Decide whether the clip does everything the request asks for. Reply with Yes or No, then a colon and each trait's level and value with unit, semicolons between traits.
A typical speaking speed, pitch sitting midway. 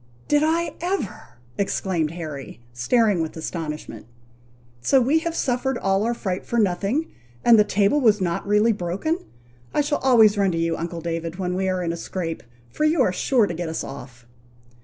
No: average, 190 wpm; high, 195 Hz